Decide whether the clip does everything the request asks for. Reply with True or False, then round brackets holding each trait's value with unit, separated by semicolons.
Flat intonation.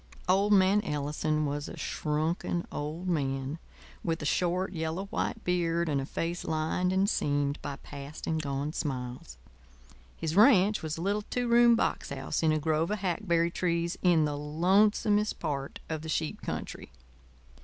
False (3.8 semitones)